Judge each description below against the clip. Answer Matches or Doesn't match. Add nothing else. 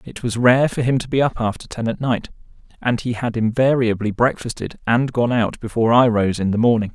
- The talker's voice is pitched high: Doesn't match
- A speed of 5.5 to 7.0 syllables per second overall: Matches